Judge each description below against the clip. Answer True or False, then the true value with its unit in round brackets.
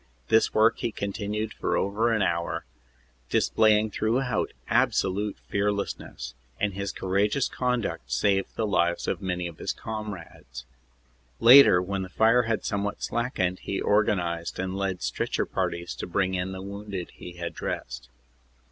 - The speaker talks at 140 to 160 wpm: True (145 wpm)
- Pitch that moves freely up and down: False (3.2 semitones)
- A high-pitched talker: False (100 Hz)